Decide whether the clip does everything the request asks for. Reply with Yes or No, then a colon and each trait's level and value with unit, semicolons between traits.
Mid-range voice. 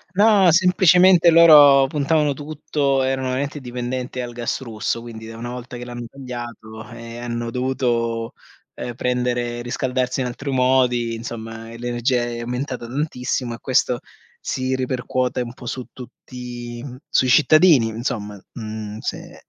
No: low, 125 Hz